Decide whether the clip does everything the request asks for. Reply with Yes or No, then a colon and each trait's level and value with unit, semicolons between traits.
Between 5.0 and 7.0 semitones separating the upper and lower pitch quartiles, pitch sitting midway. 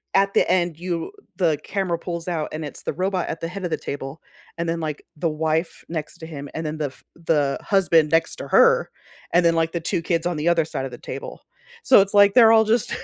No: average, 3.0 semitones; medium, 165 Hz